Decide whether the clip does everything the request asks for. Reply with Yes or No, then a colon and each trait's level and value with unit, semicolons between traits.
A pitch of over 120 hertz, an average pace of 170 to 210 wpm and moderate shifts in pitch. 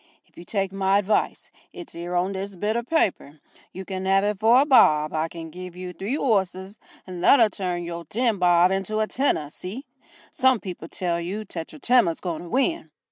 Yes: high, 190 Hz; average, 190 wpm; average, 3.7 semitones